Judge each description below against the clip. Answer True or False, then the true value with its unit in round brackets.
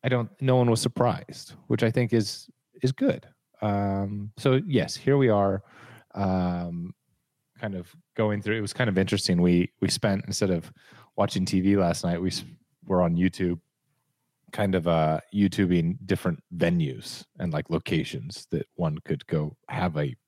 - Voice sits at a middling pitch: False (100 Hz)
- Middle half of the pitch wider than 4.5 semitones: True (5.2 semitones)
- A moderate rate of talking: True (170 wpm)